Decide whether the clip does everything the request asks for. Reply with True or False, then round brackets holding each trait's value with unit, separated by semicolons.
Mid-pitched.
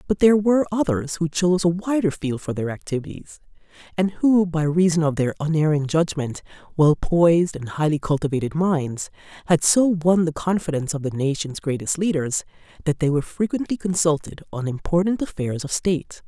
True (160 Hz)